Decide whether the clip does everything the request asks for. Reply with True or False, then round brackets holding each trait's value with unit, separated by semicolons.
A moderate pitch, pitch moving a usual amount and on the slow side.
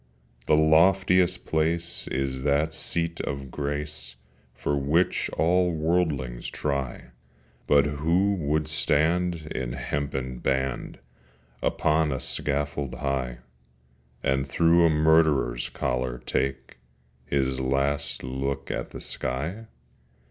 False (70 Hz; 3.2 semitones; 105 wpm)